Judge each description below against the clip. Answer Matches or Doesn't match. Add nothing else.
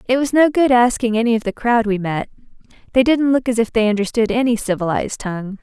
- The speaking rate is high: Matches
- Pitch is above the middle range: Matches